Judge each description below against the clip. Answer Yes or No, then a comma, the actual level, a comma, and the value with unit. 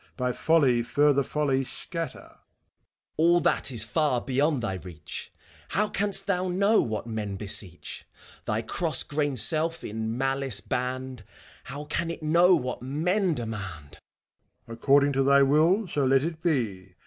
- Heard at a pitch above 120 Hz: Yes, low, 135 Hz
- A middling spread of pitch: No, wide, 5.7 semitones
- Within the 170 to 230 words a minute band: No, average, 155 wpm